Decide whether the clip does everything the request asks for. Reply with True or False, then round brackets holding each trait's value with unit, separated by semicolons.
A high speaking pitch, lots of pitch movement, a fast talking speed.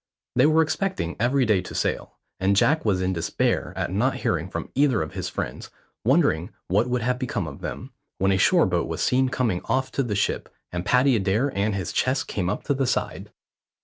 False (115 Hz; 5.9 semitones; 210 wpm)